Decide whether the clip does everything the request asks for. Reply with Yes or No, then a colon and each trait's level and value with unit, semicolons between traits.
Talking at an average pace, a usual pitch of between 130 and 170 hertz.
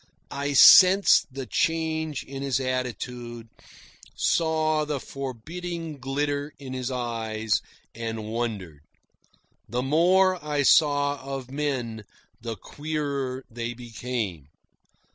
No: slow, 105 wpm; low, 135 Hz